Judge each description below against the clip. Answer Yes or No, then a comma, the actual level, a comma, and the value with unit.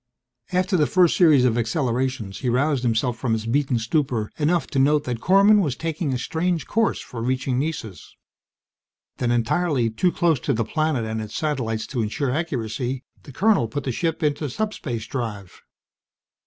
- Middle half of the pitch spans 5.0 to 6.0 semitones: Yes, average, 5.3 semitones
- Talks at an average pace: Yes, average, 170 wpm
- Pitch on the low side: Yes, low, 130 Hz